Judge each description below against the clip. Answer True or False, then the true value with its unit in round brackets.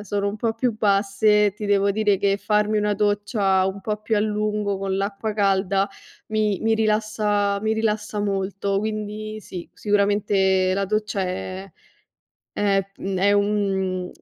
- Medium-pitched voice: False (205 Hz)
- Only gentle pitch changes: True (1.4 semitones)